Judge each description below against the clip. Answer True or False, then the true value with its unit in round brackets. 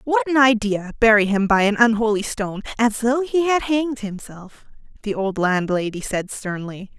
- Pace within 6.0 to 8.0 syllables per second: False (4.9 syllables/s)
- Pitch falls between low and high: False (220 Hz)